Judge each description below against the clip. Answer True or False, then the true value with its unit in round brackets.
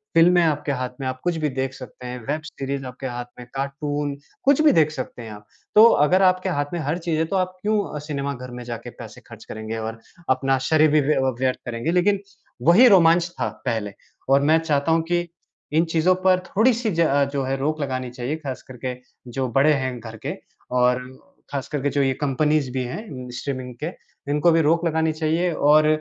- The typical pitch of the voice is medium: True (145 Hz)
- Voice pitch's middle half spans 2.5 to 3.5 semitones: False (4.3 semitones)